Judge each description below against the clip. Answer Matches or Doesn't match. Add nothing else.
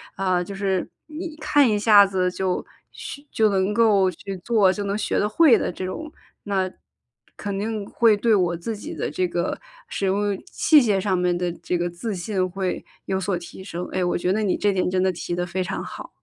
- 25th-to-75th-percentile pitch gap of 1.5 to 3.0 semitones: Matches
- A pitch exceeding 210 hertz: Doesn't match